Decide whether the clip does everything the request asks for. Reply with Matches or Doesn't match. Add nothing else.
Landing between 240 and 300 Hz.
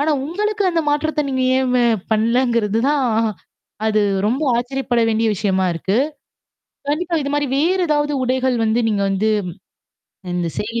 Matches